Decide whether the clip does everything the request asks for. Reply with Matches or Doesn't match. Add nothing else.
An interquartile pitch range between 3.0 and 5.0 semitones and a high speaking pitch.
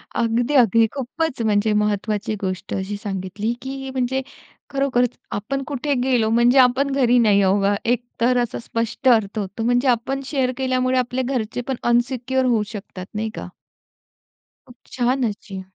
Matches